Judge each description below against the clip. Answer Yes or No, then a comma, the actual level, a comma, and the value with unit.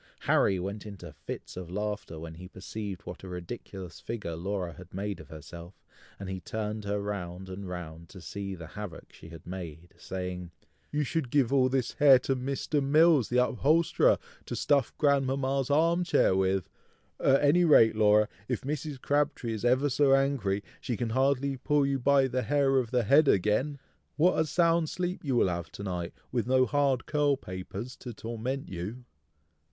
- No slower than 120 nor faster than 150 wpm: No, average, 180 wpm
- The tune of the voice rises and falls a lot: Yes, wide, 6.7 semitones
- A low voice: Yes, low, 115 Hz